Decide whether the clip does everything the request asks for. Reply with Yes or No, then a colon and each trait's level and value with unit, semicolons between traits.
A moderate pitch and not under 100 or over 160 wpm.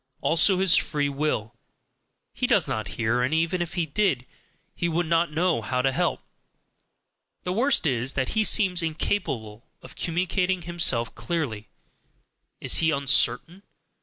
Yes: medium, 160 Hz; average, 145 wpm